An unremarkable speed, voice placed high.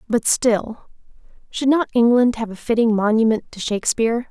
Yes: average, 155 wpm; high, 230 Hz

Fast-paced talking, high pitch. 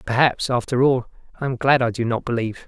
No: fast, 225 wpm; low, 125 Hz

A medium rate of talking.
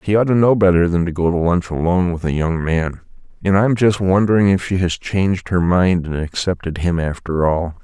No: fast, 235 wpm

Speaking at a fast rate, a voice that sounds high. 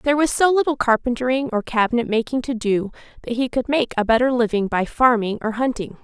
Yes: fast, 210 wpm; high, 240 Hz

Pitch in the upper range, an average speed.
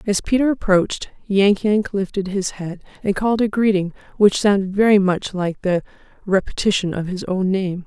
Yes: high, 195 Hz; average, 175 wpm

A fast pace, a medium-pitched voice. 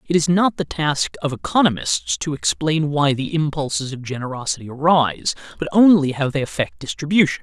No: average, 170 wpm; medium, 150 Hz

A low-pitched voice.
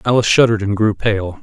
Yes: low, 105 Hz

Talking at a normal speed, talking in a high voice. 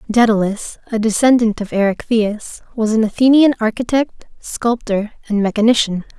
No: slow, 115 wpm; high, 225 Hz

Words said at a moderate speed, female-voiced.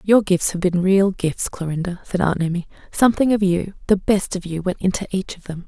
No: fast, 210 wpm; female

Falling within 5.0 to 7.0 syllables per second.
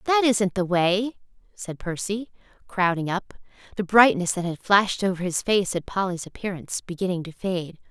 Yes: 5.1 syllables/s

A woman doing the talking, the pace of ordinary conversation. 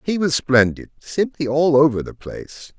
No: male; average, 170 wpm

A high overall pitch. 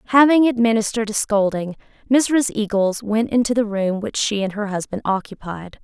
Yes: high, 215 Hz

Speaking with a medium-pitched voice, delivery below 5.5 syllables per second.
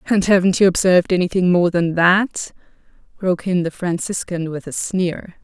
Yes: medium, 180 Hz; 5.0 syllables/s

